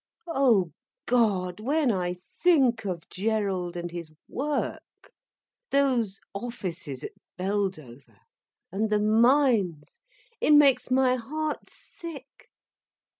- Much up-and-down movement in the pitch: Yes, wide, 6.9 semitones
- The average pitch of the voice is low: No, high, 220 Hz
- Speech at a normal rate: No, slow, 90 wpm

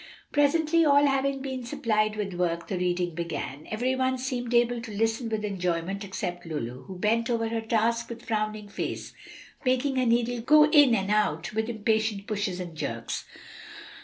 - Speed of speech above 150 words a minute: Yes, average, 170 wpm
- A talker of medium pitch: No, high, 220 Hz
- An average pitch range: Yes, average, 4.3 semitones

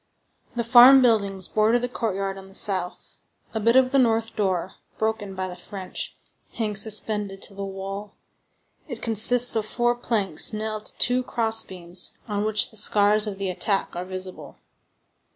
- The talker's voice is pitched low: No, high, 210 Hz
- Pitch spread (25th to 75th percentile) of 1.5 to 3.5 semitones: Yes, average, 2.8 semitones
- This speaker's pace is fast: No, average, 170 wpm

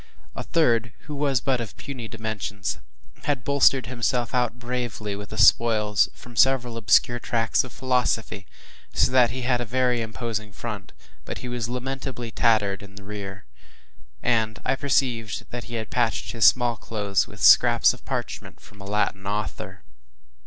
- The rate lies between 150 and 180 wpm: Yes, average, 160 wpm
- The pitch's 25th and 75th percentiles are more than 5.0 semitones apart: No, average, 2.9 semitones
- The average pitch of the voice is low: Yes, low, 115 Hz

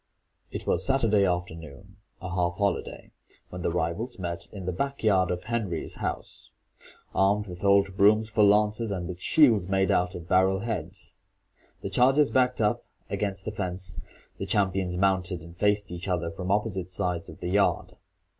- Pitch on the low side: Yes, very low, 95 Hz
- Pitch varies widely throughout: No, average, 2.8 semitones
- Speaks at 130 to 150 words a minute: No, average, 170 wpm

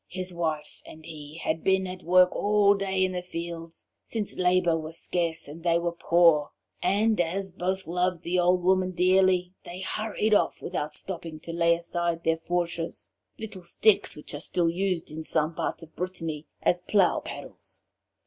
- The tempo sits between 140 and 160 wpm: No, average, 175 wpm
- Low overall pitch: No, medium, 175 Hz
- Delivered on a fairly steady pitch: Yes, narrow, 2.1 semitones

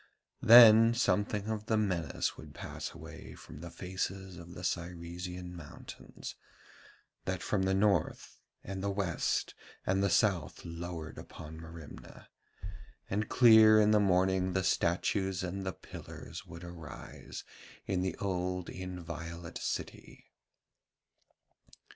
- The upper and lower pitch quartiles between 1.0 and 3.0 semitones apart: Yes, narrow, 2.6 semitones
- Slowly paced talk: Yes, slow, 125 wpm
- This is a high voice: No, very low, 95 Hz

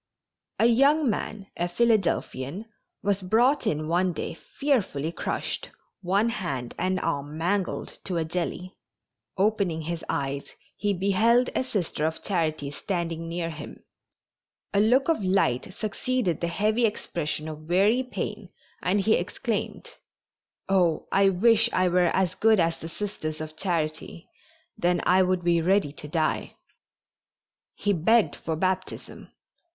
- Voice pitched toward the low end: No, medium, 185 Hz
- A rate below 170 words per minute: Yes, average, 140 wpm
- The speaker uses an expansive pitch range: No, average, 4.2 semitones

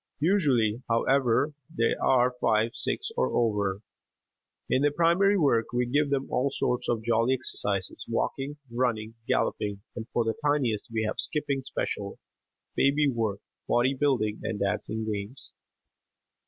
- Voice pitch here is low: Yes, low, 120 Hz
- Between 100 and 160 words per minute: Yes, average, 140 wpm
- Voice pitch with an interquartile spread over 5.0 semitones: No, average, 4.1 semitones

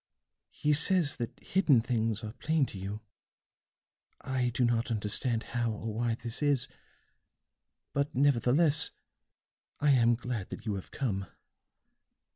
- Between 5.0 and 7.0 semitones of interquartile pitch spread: No, average, 4.0 semitones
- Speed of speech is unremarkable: No, slow, 130 wpm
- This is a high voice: No, low, 120 Hz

